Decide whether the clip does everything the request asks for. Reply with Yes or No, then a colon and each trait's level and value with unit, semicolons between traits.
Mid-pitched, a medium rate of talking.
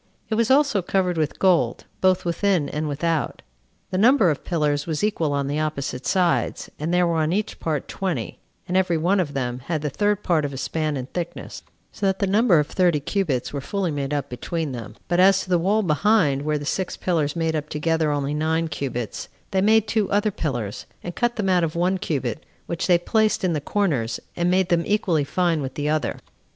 No: medium, 165 Hz; fast, 215 wpm